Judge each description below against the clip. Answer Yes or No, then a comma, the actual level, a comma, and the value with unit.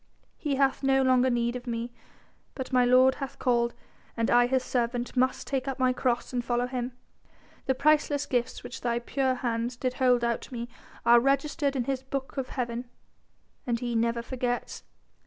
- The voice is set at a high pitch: Yes, very high, 250 Hz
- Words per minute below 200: Yes, average, 185 wpm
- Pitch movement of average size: No, narrow, 1.8 semitones